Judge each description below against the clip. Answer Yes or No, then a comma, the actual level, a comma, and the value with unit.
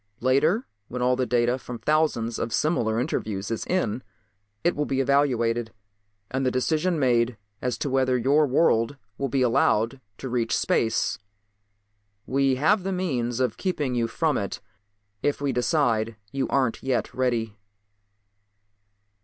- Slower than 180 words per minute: Yes, average, 145 wpm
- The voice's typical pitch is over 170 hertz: No, low, 130 Hz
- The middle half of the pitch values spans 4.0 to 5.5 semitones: No, average, 3.5 semitones